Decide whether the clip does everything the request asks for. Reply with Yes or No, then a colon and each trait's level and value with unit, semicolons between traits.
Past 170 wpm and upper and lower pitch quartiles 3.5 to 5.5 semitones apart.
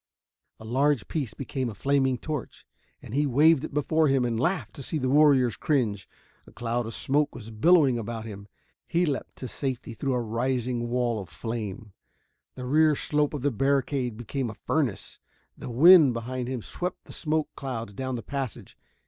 Yes: average, 180 wpm; average, 3.8 semitones